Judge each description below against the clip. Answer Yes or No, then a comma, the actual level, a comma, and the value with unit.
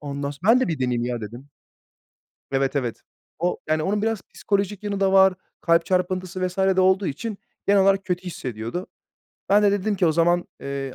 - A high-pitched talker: No, medium, 180 Hz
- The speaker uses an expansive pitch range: Yes, wide, 5.7 semitones